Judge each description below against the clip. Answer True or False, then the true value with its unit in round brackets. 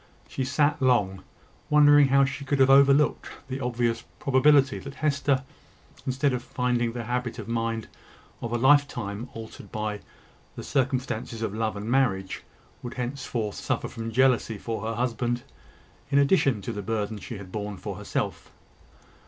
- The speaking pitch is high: False (125 Hz)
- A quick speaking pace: False (155 wpm)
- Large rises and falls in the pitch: False (3.2 semitones)